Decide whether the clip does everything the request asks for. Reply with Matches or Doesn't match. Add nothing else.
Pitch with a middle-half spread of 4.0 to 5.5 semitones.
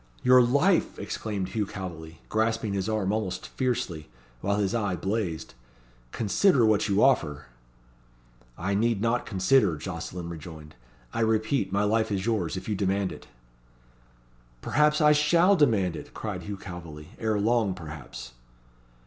Matches